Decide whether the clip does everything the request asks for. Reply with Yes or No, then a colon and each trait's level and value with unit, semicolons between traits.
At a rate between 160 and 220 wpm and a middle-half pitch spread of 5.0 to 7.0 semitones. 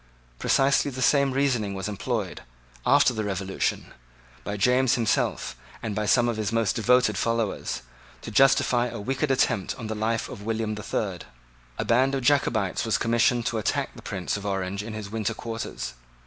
No: average, 175 wpm; average, 3.3 semitones